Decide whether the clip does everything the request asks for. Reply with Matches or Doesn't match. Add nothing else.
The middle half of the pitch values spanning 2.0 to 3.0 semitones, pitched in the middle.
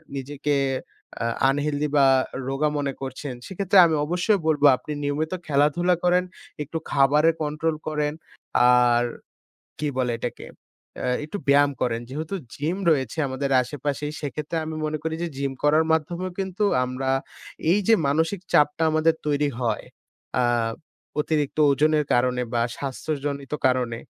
Matches